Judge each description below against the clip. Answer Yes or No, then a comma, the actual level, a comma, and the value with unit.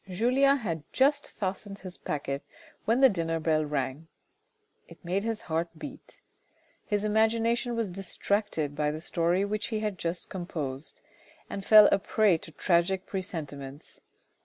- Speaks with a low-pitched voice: No, medium, 185 Hz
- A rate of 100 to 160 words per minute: Yes, average, 145 wpm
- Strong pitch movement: No, average, 4.9 semitones